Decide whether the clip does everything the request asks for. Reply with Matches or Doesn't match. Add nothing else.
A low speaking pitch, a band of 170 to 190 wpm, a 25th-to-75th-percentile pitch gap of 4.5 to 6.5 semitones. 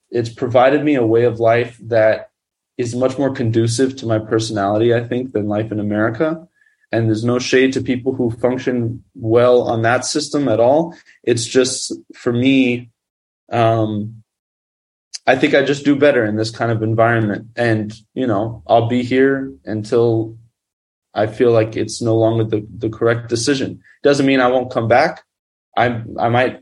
Doesn't match